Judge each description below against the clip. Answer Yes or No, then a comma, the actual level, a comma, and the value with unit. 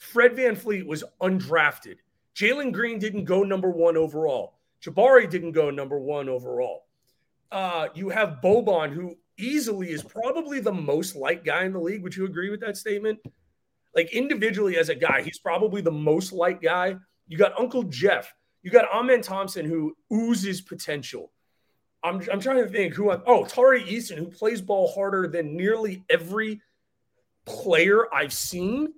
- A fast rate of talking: No, average, 170 wpm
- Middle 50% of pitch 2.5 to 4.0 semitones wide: No, average, 5.0 semitones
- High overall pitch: Yes, high, 195 Hz